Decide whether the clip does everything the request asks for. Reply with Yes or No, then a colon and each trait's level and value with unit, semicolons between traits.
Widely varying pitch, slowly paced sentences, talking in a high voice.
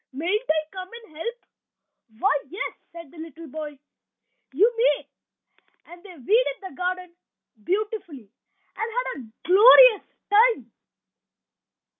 Yes: wide, 5.7 semitones; slow, 120 wpm; very high, 365 Hz